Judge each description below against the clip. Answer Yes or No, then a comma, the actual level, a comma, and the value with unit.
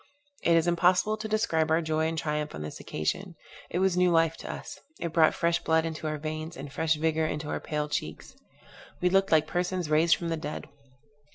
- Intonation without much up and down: Yes, narrow, 2.0 semitones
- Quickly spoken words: Yes, fast, 210 wpm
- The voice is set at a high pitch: No, medium, 160 Hz